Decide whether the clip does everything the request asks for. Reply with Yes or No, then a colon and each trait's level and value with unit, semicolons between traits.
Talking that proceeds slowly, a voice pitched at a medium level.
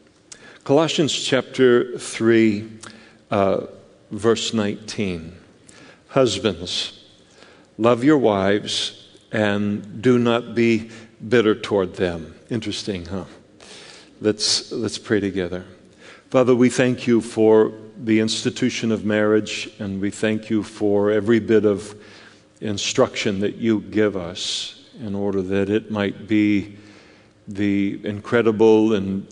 No: slow, 110 wpm; low, 105 Hz